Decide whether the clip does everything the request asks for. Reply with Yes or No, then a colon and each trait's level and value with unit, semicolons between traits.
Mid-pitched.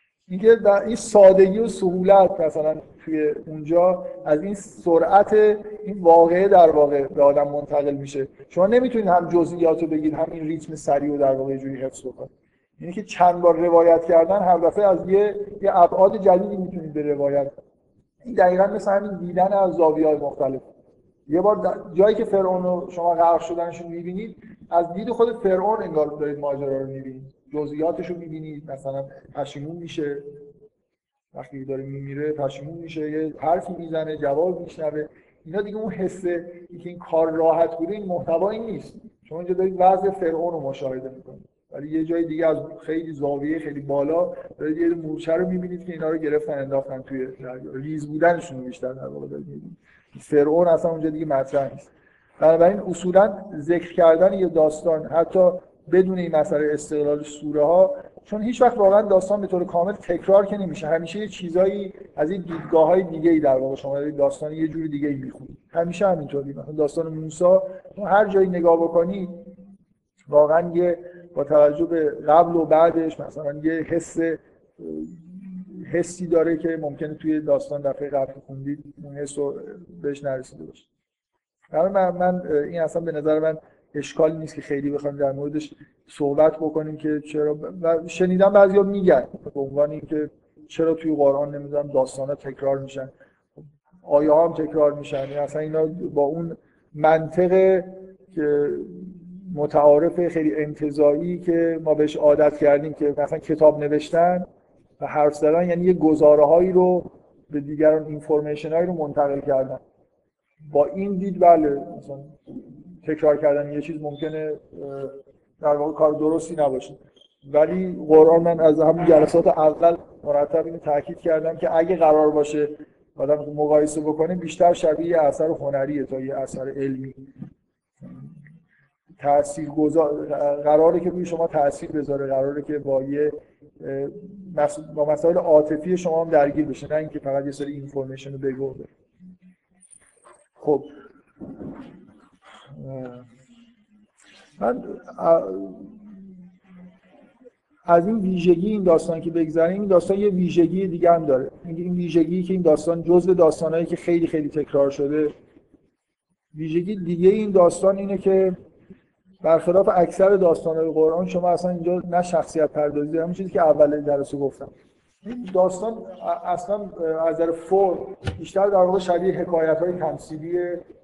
Yes: medium, 160 Hz